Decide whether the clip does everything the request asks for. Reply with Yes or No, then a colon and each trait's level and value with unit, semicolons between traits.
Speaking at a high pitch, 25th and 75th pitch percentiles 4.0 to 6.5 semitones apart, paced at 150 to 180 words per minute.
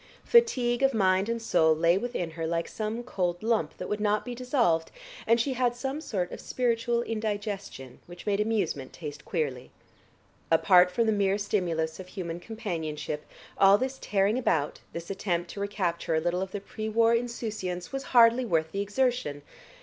Yes: high, 200 Hz; average, 5.3 semitones; average, 175 wpm